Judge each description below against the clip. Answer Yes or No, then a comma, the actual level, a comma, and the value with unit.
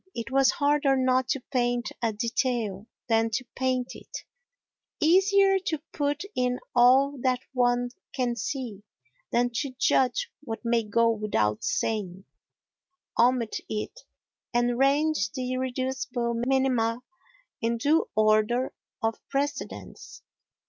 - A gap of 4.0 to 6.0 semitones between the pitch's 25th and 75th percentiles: No, average, 2.8 semitones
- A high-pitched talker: Yes, very high, 250 Hz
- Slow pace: Yes, slow, 120 wpm